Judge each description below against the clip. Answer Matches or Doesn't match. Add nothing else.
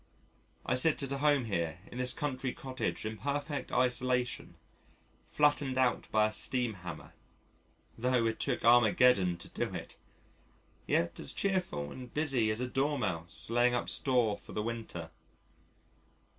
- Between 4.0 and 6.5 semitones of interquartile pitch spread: Doesn't match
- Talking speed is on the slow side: Doesn't match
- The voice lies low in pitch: Matches